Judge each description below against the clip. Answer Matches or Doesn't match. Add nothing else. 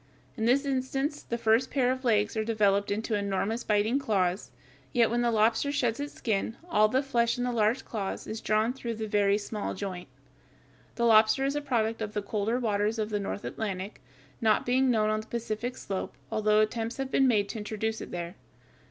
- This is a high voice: Matches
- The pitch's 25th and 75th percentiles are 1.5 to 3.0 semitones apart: Matches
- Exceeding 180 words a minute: Matches